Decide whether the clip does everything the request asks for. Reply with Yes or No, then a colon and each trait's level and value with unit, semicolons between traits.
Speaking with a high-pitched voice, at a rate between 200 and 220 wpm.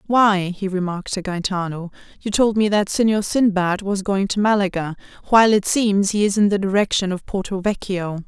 No: high, 195 Hz; average, 190 wpm